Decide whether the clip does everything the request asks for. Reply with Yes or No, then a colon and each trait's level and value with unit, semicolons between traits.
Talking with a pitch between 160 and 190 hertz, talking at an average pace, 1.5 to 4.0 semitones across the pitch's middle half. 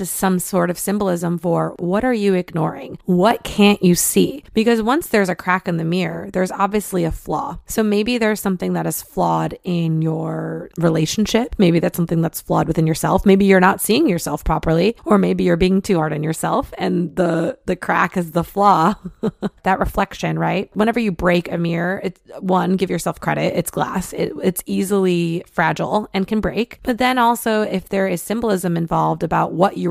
Yes: medium, 185 Hz; average, 195 wpm; average, 2.9 semitones